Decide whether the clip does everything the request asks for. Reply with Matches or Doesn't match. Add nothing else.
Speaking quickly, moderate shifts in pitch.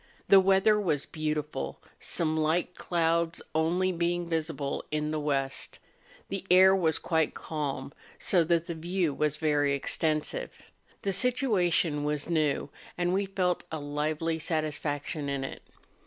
Doesn't match